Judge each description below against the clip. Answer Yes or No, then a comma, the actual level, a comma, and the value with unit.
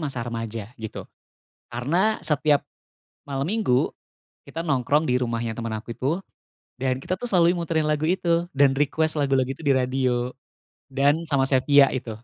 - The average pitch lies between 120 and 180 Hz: Yes, medium, 140 Hz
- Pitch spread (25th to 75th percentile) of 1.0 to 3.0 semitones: No, average, 4.1 semitones